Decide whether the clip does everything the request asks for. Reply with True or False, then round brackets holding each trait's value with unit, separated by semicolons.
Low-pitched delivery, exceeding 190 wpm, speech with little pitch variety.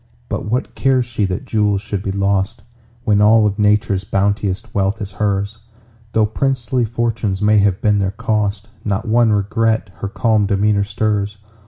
False (105 Hz; 165 wpm; 1.9 semitones)